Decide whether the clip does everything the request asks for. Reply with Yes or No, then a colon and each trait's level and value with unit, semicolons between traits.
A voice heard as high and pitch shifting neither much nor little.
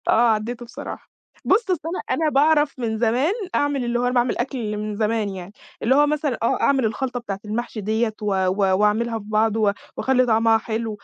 Yes: high, 230 Hz; average, 3.5 semitones